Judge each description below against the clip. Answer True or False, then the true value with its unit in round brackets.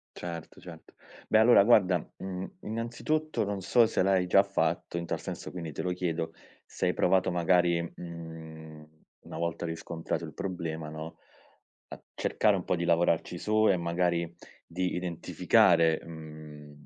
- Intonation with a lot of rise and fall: False (2.4 semitones)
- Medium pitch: False (85 Hz)